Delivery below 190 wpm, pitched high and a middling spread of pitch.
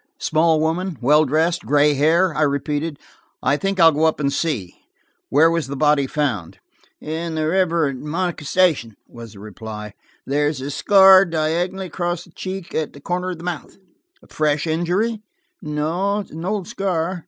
No: average, 175 wpm; medium, 160 Hz; average, 3.4 semitones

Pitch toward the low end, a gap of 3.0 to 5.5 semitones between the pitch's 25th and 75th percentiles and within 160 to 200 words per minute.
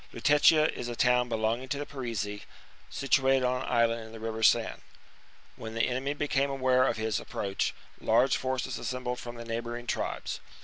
No: low, 125 Hz; narrow, 2.4 semitones; average, 185 wpm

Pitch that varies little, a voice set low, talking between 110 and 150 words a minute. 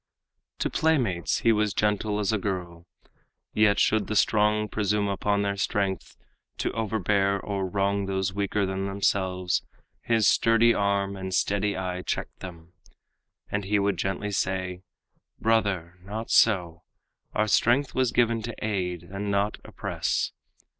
Yes: narrow, 2.1 semitones; low, 100 Hz; average, 140 wpm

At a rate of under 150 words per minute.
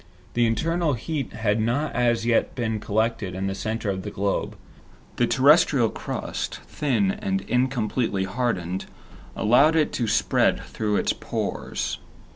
Yes: average, 140 wpm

